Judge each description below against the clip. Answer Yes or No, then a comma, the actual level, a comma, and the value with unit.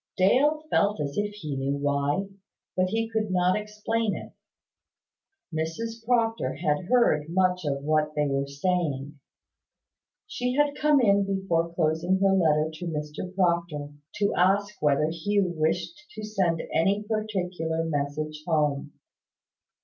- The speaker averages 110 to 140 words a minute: Yes, slow, 135 wpm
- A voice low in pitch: No, medium, 180 Hz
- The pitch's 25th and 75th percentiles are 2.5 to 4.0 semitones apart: No, average, 5.3 semitones